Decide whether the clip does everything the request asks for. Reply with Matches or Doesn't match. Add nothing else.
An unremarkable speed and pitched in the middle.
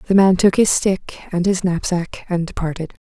Matches